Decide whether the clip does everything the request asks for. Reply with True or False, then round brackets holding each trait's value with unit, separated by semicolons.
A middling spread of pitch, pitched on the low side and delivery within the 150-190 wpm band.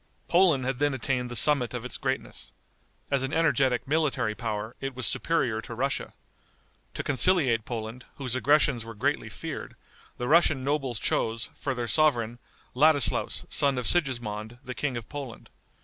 True (3.4 semitones; 130 Hz; 160 wpm)